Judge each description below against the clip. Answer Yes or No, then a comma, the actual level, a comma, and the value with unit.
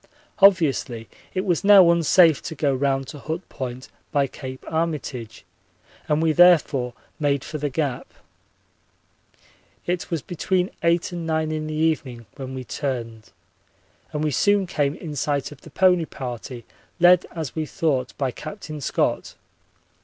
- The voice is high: No, medium, 155 Hz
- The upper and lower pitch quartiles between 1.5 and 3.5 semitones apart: No, average, 4.1 semitones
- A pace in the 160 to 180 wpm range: No, average, 150 wpm